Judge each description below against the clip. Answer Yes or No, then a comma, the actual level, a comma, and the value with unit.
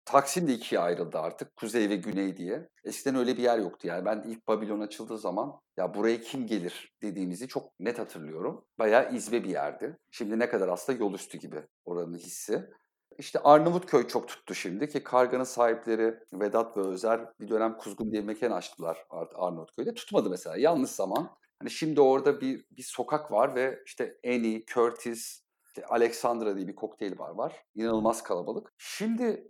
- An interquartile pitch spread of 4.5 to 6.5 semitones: No, average, 3.3 semitones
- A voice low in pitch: Yes, low, 115 Hz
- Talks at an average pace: No, fast, 175 wpm